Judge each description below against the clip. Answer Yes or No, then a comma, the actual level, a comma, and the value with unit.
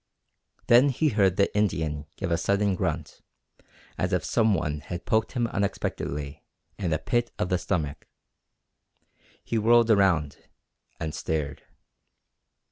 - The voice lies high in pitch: No, very low, 90 Hz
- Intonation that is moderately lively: No, wide, 5.7 semitones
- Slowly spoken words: Yes, slow, 130 wpm